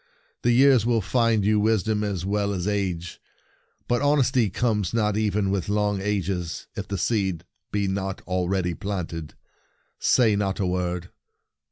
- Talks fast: No, average, 165 wpm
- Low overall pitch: Yes, low, 100 Hz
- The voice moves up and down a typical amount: Yes, average, 3.0 semitones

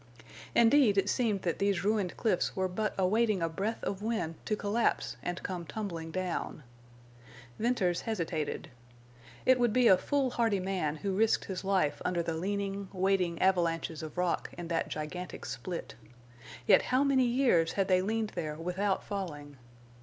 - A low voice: No, high, 190 Hz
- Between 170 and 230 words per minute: No, average, 160 wpm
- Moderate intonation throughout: Yes, average, 4.0 semitones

